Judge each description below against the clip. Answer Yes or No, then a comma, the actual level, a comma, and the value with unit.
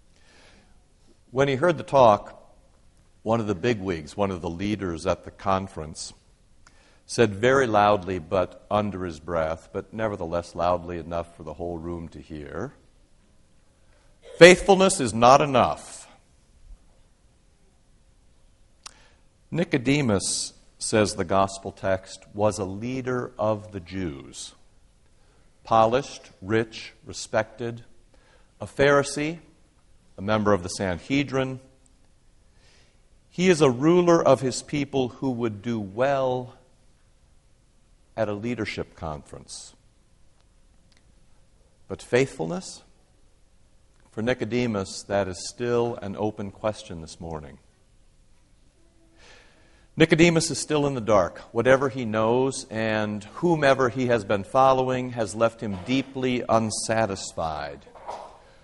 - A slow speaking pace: Yes, slow, 105 wpm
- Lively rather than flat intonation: Yes, wide, 6.1 semitones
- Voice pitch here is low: Yes, low, 105 Hz